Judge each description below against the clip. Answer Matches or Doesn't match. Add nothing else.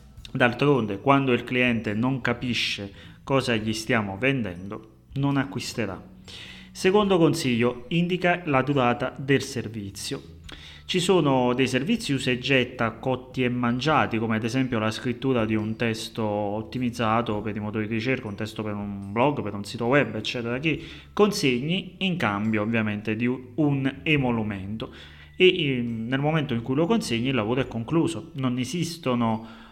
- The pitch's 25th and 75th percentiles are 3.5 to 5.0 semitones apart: Matches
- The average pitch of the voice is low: Matches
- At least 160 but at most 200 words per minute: Doesn't match